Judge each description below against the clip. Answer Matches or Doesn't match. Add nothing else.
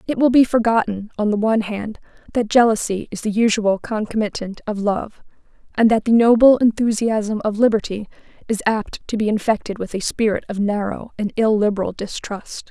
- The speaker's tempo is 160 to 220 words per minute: Matches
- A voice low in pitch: Doesn't match